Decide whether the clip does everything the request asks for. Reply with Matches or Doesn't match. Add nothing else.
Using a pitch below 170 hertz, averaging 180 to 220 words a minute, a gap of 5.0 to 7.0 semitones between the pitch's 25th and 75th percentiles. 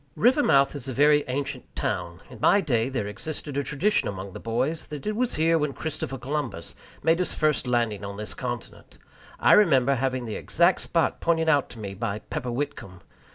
Matches